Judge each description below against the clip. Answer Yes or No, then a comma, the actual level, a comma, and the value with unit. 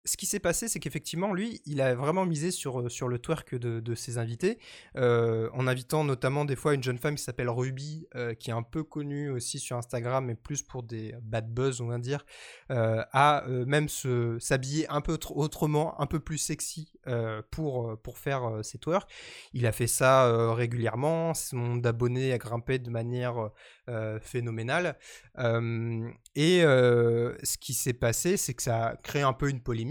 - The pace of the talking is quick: No, average, 200 wpm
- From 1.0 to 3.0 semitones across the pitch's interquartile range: No, average, 4.0 semitones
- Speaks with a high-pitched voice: No, low, 130 Hz